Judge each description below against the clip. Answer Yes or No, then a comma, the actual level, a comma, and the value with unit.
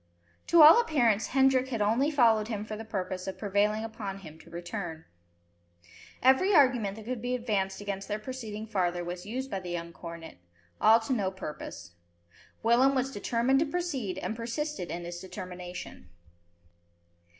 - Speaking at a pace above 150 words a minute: Yes, average, 160 wpm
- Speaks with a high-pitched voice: Yes, high, 215 Hz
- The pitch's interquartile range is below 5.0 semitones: No, wide, 5.4 semitones